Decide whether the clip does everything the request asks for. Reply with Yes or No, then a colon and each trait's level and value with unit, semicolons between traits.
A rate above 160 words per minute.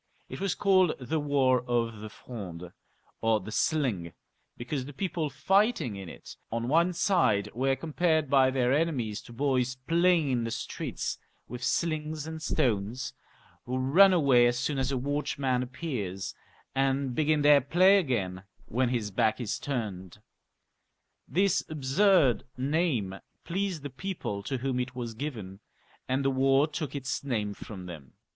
No: average, 155 wpm